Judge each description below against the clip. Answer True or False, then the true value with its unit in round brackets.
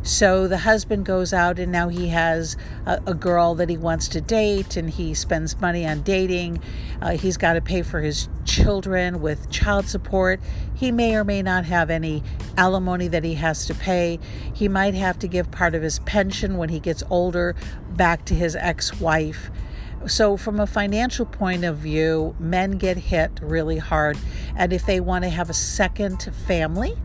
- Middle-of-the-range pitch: True (175 Hz)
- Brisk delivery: False (190 wpm)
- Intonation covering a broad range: False (2.8 semitones)